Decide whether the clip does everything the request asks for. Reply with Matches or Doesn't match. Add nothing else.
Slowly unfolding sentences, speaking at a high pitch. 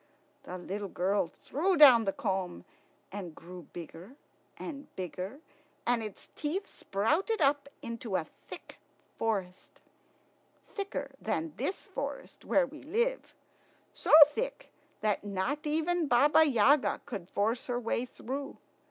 Matches